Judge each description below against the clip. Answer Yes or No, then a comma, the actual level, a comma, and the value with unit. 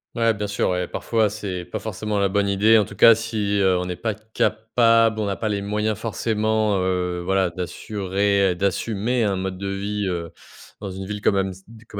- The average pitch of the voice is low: Yes, low, 100 Hz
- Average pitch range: No, narrow, 2.2 semitones